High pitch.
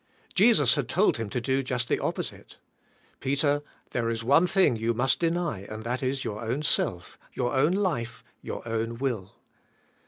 No: low, 125 Hz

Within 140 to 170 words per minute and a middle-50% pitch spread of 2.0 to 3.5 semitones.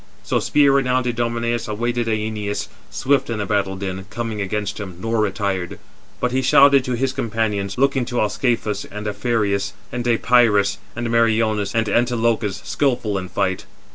Yes: average, 155 wpm; average, 2.9 semitones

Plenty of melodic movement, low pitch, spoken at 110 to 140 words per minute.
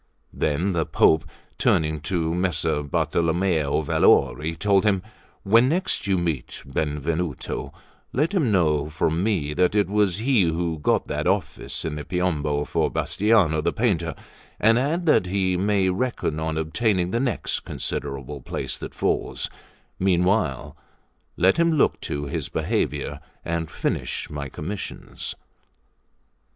No: average, 4.8 semitones; very low, 85 Hz; slow, 135 wpm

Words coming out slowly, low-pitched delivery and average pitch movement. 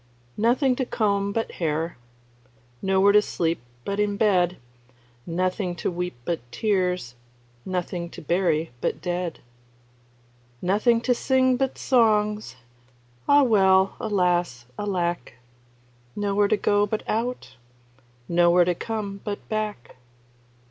No: slow, 115 wpm; high, 195 Hz; average, 3.4 semitones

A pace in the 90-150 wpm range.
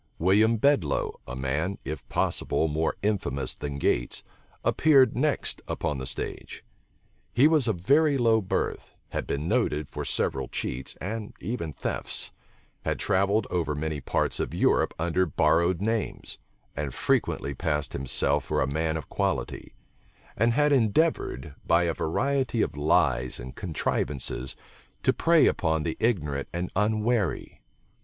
Yes: average, 140 wpm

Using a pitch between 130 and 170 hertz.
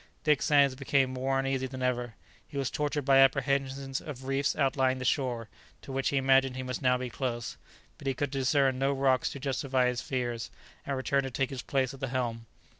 Yes: low, 135 Hz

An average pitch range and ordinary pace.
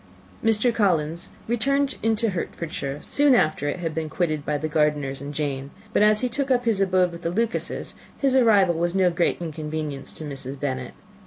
No: wide, 6.7 semitones; average, 185 wpm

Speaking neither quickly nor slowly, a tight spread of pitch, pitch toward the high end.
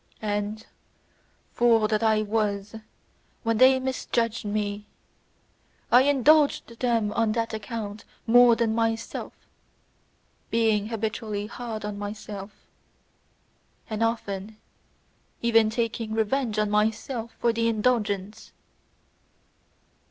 No: slow, 100 wpm; narrow, 1.7 semitones; high, 220 Hz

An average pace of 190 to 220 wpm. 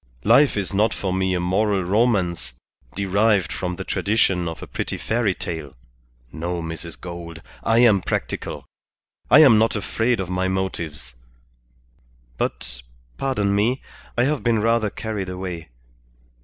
No: average, 140 wpm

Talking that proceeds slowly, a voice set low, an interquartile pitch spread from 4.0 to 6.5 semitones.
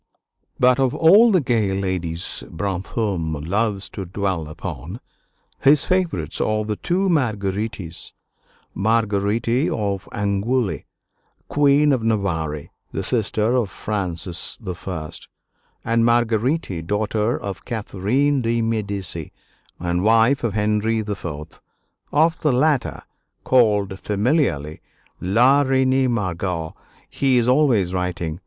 Yes: slow, 110 wpm; low, 105 Hz; average, 5.1 semitones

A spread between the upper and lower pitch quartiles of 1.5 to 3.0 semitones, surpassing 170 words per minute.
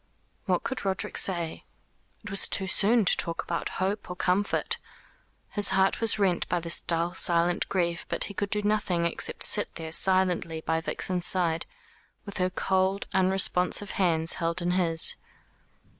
No: narrow, 2.5 semitones; average, 160 wpm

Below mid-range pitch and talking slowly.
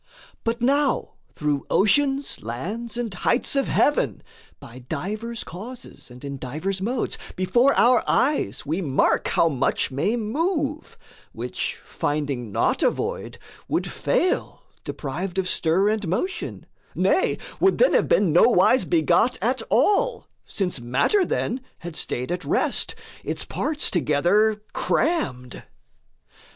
No: high, 200 Hz; slow, 130 wpm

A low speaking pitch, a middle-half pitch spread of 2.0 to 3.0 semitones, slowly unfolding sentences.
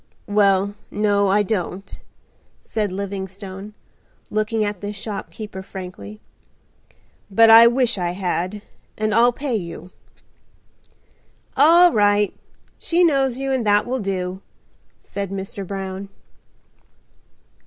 No: high, 205 Hz; average, 2.7 semitones; slow, 110 wpm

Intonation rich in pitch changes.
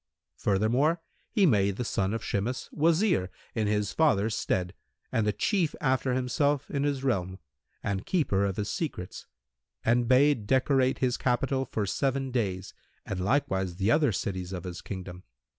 Yes: wide, 5.9 semitones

